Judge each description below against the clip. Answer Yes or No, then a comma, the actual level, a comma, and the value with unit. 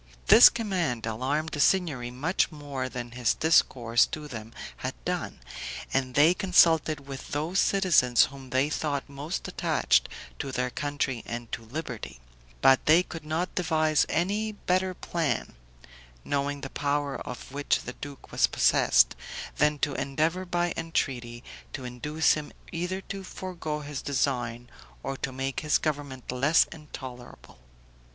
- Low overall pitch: No, medium, 145 Hz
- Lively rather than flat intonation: No, average, 4.1 semitones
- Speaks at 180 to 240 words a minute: No, average, 145 wpm